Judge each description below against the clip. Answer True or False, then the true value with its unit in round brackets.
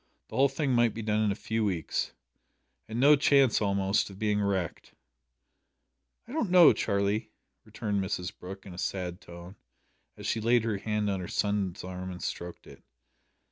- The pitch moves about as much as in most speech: True (3.1 semitones)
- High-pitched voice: False (105 Hz)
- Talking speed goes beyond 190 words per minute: False (180 wpm)